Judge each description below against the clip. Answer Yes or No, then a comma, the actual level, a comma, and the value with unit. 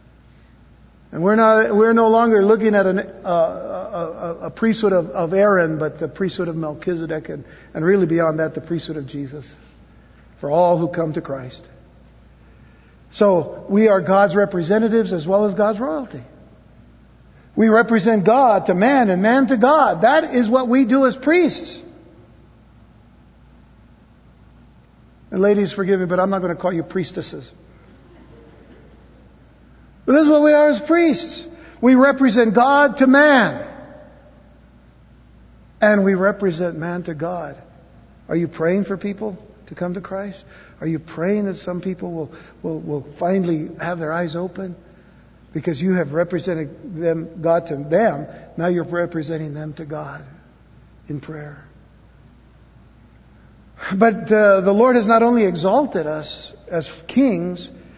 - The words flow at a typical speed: Yes, average, 150 wpm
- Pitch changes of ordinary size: Yes, average, 5.0 semitones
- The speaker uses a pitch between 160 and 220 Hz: Yes, medium, 185 Hz